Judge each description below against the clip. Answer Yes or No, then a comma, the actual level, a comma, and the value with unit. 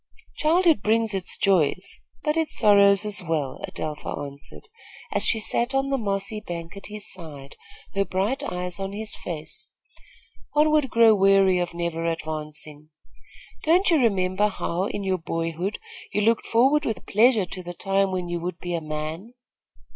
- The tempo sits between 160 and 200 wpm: Yes, average, 165 wpm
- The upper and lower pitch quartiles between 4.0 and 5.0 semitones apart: Yes, average, 4.5 semitones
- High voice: Yes, high, 195 Hz